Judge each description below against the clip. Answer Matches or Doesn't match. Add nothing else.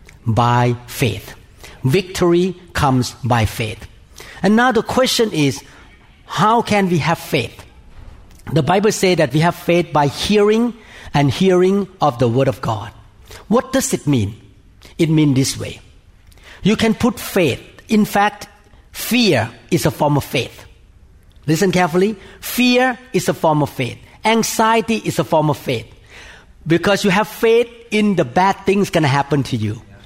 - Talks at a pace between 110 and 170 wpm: Matches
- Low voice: Doesn't match